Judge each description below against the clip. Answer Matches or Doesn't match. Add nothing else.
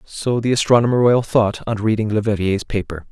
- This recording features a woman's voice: Doesn't match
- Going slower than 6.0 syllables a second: Matches